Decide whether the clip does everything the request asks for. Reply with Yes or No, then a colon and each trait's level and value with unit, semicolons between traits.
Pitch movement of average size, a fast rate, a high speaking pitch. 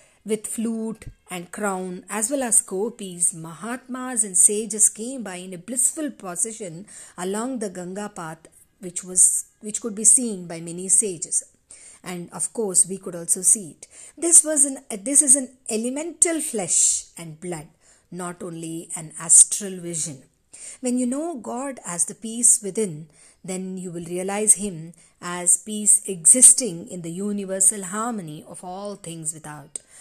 Yes: average, 4.4 semitones; fast, 155 wpm; high, 195 Hz